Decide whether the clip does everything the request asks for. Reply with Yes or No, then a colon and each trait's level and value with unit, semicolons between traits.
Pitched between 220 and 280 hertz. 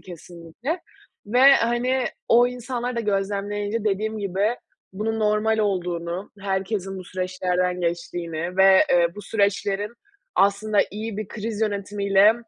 No: high, 205 Hz